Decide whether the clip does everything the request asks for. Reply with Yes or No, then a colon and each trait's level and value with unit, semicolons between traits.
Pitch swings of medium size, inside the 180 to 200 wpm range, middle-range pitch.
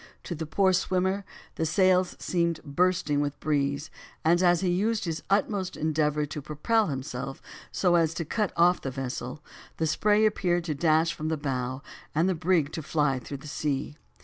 Yes: average, 3.9 semitones; average, 185 wpm; medium, 160 Hz